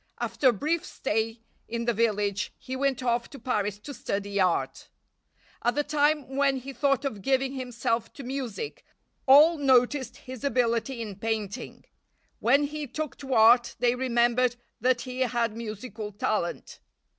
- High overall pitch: Yes, high, 245 Hz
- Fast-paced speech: No, average, 155 wpm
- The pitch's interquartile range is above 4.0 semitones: No, average, 3.2 semitones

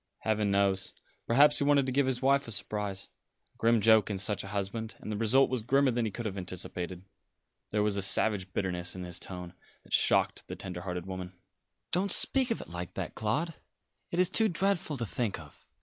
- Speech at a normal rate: No, fast, 210 wpm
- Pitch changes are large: Yes, wide, 5.7 semitones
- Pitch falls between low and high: No, low, 105 Hz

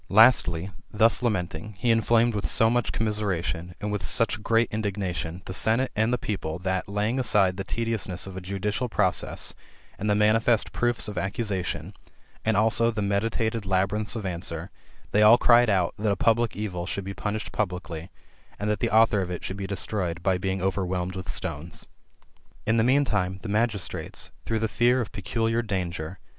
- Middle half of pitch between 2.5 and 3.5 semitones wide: Yes, average, 3.2 semitones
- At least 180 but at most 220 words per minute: Yes, average, 185 wpm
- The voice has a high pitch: No, low, 105 Hz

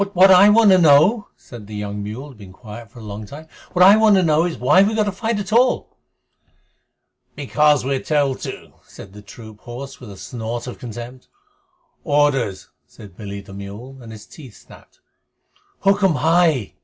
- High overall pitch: No, low, 135 Hz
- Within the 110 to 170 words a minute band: No, average, 190 wpm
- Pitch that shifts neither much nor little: No, wide, 8.6 semitones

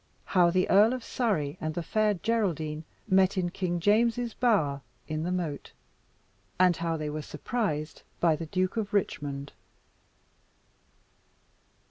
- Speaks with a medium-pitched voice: Yes, medium, 180 Hz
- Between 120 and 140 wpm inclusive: Yes, slow, 135 wpm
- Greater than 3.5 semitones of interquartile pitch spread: Yes, average, 5.2 semitones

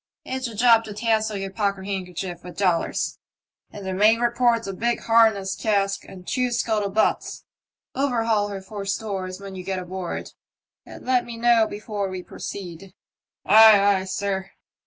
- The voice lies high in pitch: Yes, high, 200 Hz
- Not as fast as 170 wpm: Yes, average, 160 wpm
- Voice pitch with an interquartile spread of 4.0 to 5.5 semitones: No, average, 3.0 semitones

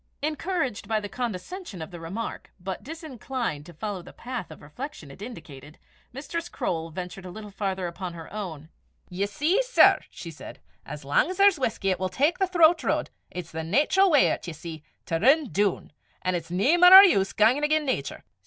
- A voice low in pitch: No, high, 205 Hz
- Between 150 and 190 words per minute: No, average, 200 wpm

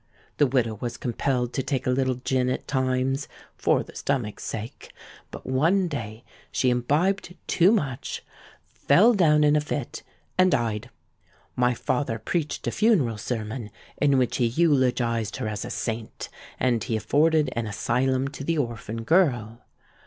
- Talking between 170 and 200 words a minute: No, average, 155 wpm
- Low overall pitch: Yes, low, 130 Hz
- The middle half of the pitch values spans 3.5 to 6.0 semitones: Yes, average, 3.9 semitones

